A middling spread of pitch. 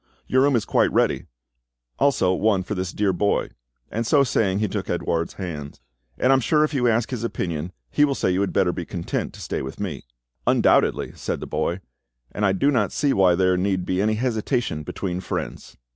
Yes: average, 5.0 semitones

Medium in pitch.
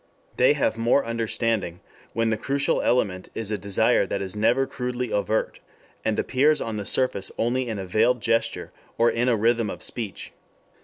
No: low, 115 Hz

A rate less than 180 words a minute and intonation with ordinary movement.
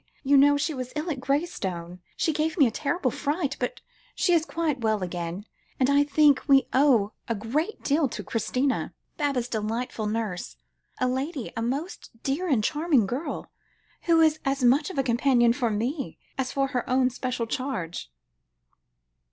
Yes: average, 170 wpm; average, 4.1 semitones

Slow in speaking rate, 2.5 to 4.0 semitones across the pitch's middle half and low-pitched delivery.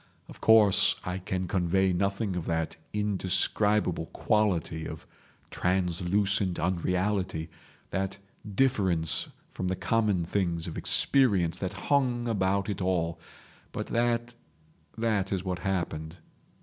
Yes: slow, 110 wpm; average, 3.1 semitones; very low, 95 Hz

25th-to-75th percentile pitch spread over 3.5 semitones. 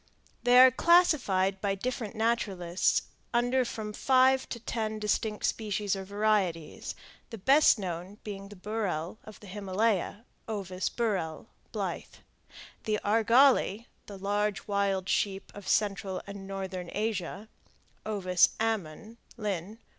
No: average, 2.7 semitones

